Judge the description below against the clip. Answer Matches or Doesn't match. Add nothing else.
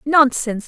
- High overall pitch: Matches